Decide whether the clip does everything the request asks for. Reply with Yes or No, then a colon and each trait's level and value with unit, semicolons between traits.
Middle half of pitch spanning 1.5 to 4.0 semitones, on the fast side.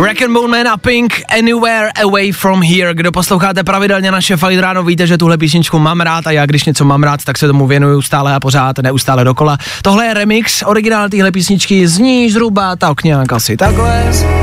No: wide, 5.8 semitones; fast, 200 wpm